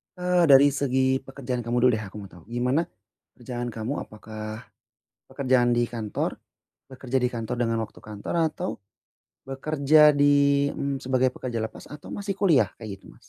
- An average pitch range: Yes, average, 3.4 semitones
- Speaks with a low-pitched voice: Yes, low, 130 Hz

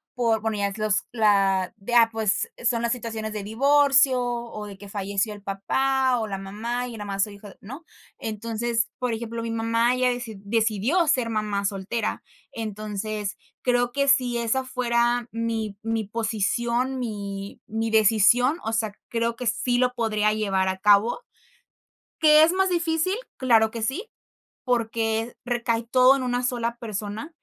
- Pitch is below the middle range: No, high, 230 Hz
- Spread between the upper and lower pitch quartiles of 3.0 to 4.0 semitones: No, narrow, 2.6 semitones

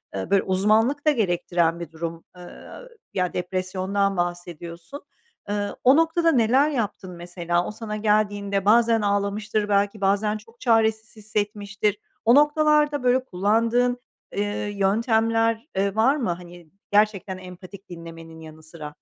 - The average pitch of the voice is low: No, high, 205 Hz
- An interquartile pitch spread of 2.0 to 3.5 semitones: No, average, 4.0 semitones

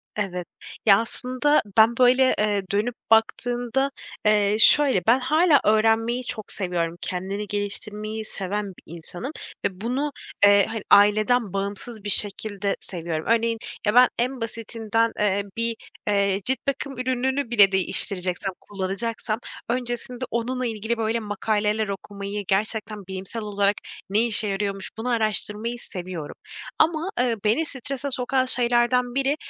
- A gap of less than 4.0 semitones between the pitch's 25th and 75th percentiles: Yes, average, 3.4 semitones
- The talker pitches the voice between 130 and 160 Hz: No, high, 220 Hz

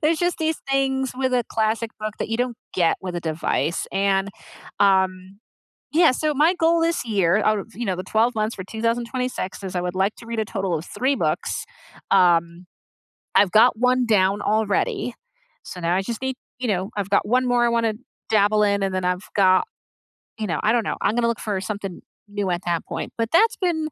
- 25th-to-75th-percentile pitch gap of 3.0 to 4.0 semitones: No, average, 4.5 semitones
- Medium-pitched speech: No, high, 215 Hz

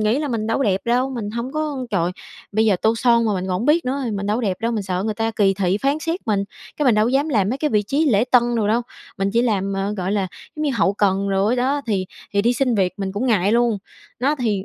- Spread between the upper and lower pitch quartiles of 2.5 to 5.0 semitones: Yes, average, 4.1 semitones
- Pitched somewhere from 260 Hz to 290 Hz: No, high, 220 Hz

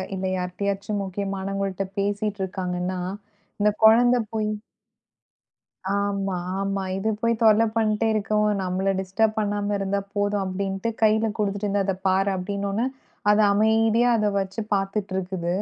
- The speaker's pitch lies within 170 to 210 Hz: Yes, high, 200 Hz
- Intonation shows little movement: Yes, narrow, 1.7 semitones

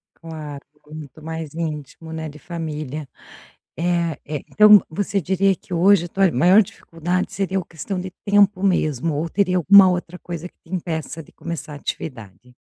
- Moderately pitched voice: Yes, medium, 165 Hz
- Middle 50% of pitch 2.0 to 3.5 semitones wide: Yes, average, 3.2 semitones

